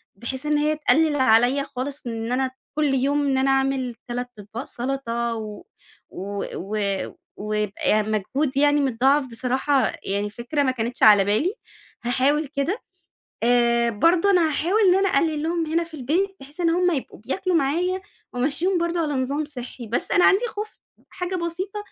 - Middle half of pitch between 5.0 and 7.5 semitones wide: Yes, average, 5.3 semitones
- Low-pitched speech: No, very high, 275 Hz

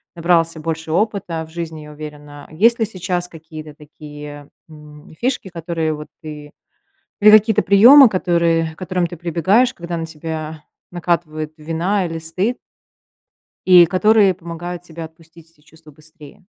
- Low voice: No, medium, 165 Hz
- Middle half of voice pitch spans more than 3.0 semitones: No, narrow, 2.6 semitones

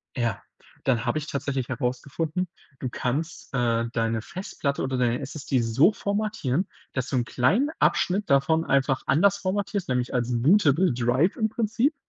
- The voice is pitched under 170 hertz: Yes, medium, 140 Hz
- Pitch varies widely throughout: Yes, wide, 7.1 semitones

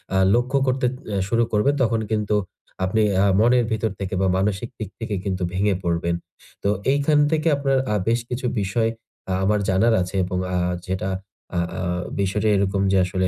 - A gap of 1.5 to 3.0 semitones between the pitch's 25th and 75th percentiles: No, average, 3.7 semitones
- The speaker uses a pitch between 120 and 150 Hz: No, low, 105 Hz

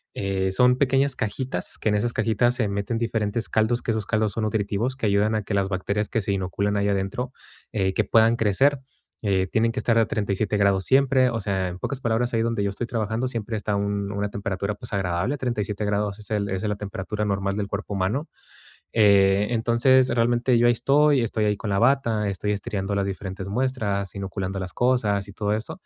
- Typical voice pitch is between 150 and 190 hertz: No, low, 105 Hz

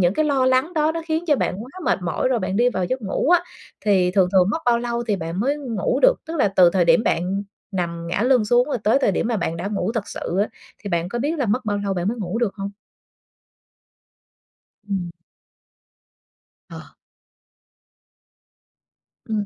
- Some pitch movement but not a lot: No, wide, 5.7 semitones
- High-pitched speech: Yes, high, 210 Hz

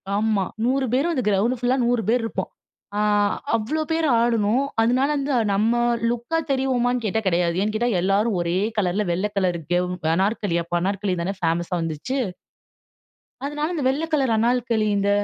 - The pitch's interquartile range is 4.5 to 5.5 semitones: Yes, average, 4.8 semitones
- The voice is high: Yes, high, 225 Hz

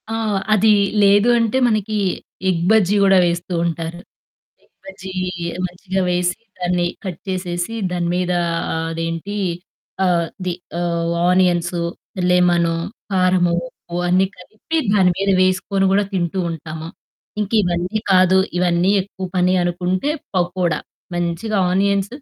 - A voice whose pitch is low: No, medium, 180 Hz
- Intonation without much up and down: Yes, narrow, 1.8 semitones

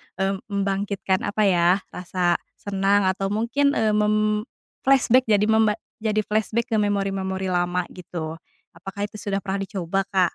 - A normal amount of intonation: No, narrow, 2.0 semitones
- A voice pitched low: No, high, 200 Hz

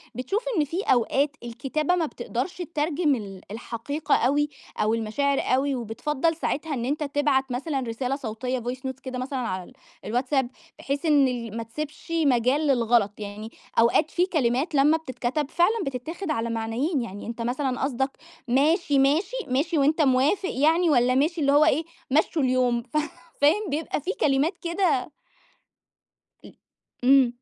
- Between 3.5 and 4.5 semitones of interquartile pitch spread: Yes, average, 3.9 semitones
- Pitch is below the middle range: No, very high, 275 Hz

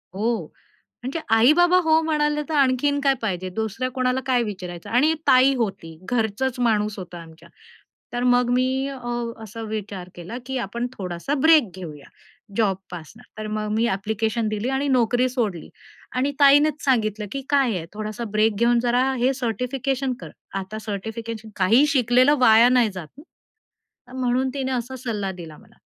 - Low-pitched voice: No, high, 235 Hz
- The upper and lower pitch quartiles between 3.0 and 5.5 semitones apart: Yes, average, 3.9 semitones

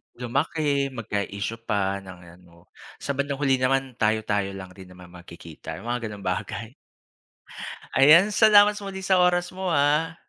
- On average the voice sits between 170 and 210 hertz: No, low, 120 Hz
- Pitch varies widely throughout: Yes, wide, 7.9 semitones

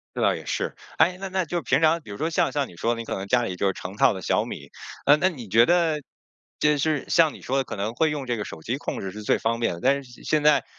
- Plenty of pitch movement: Yes, wide, 5.9 semitones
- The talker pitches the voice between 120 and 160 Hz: Yes, low, 135 Hz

